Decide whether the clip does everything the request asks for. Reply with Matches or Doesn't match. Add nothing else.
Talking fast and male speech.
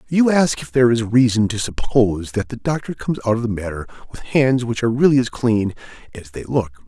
Matches